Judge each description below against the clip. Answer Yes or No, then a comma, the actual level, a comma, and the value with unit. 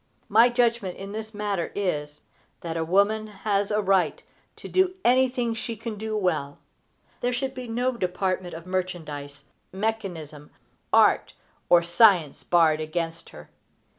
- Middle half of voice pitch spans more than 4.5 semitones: Yes, average, 5.0 semitones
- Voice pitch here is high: Yes, high, 195 Hz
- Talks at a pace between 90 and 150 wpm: Yes, average, 140 wpm